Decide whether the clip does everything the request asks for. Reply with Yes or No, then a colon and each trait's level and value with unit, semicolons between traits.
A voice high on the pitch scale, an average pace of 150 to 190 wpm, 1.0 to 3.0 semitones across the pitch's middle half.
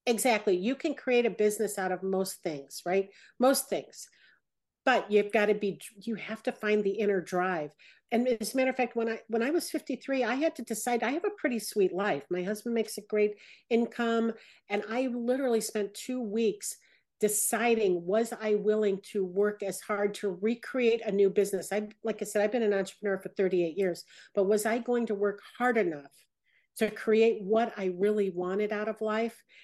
No: high, 215 Hz; average, 200 wpm; average, 2.7 semitones